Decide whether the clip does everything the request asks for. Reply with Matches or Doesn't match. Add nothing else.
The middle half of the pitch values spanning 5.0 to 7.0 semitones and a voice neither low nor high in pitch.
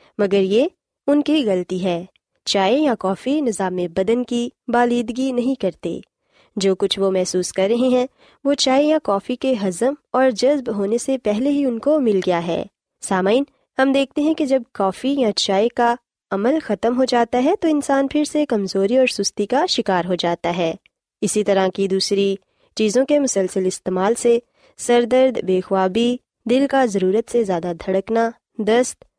Doesn't match